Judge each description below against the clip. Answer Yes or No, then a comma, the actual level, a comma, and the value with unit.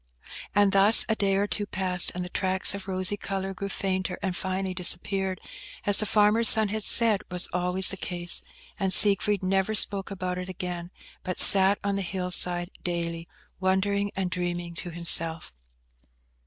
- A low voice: No, high, 190 Hz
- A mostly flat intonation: Yes, narrow, 1.8 semitones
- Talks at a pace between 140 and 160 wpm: No, average, 170 wpm